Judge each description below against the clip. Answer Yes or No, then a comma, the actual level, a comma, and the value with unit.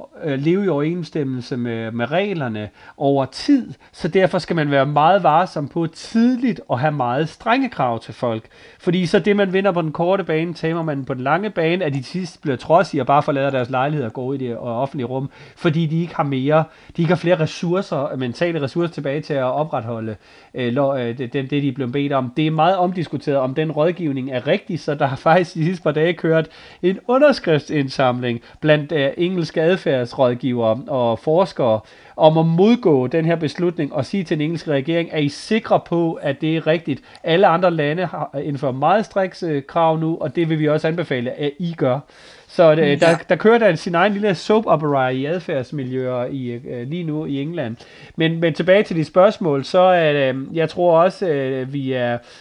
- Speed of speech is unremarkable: Yes, average, 205 wpm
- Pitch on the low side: No, medium, 155 Hz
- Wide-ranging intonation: No, average, 4.2 semitones